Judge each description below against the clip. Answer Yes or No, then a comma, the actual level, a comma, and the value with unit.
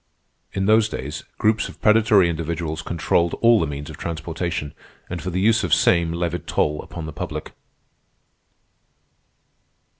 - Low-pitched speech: Yes, very low, 85 Hz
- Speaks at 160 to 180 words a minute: No, average, 150 wpm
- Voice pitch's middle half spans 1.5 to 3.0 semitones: No, average, 3.5 semitones